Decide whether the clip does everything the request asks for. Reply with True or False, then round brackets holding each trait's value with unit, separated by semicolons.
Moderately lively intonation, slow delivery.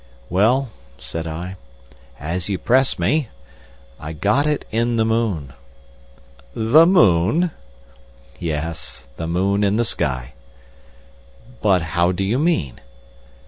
False (6.3 semitones; 110 wpm)